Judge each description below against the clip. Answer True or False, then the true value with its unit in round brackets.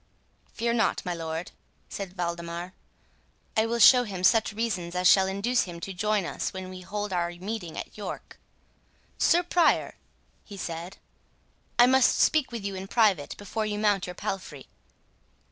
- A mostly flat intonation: False (3.8 semitones)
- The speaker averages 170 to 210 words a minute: False (160 wpm)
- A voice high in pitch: True (195 Hz)